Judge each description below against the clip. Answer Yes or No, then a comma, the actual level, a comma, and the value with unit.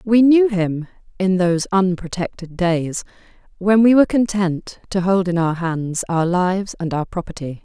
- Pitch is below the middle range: No, medium, 185 Hz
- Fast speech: No, average, 165 wpm